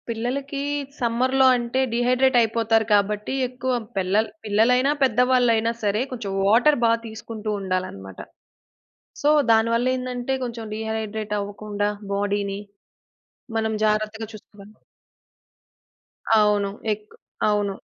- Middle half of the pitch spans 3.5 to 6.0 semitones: No, average, 2.9 semitones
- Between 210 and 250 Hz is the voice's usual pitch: Yes, high, 220 Hz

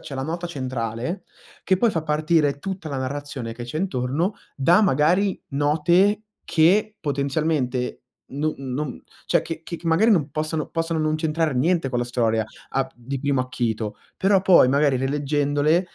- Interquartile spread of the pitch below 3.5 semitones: No, average, 4.1 semitones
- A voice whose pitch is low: No, medium, 150 Hz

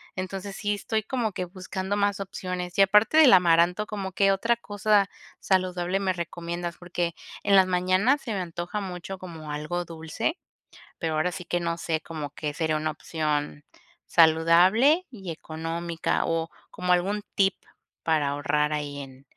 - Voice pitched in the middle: Yes, medium, 180 Hz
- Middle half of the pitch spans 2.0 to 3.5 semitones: Yes, average, 3.2 semitones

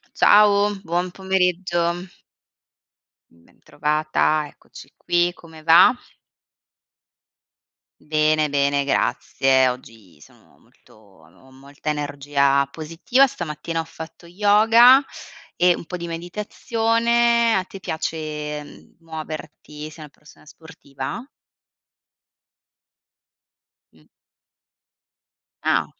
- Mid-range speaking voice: Yes, medium, 160 Hz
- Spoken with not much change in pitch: No, average, 4.1 semitones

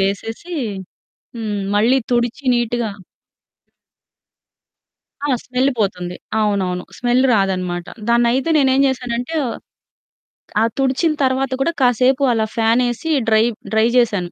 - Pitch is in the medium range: No, high, 235 Hz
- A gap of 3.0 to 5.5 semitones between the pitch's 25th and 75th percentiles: Yes, average, 3.8 semitones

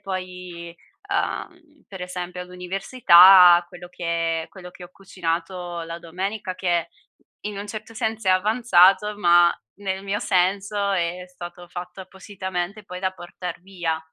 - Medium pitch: Yes, medium, 180 Hz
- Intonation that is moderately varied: No, narrow, 2.0 semitones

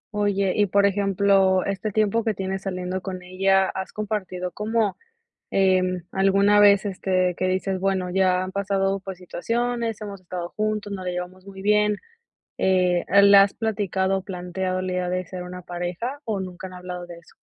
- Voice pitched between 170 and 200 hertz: Yes, high, 190 Hz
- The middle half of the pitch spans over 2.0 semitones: No, narrow, 1.7 semitones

